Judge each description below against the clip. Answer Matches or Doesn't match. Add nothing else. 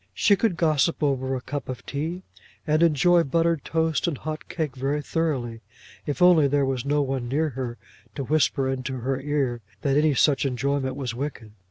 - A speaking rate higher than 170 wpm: Matches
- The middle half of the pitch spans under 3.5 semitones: Matches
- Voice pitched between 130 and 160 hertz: Matches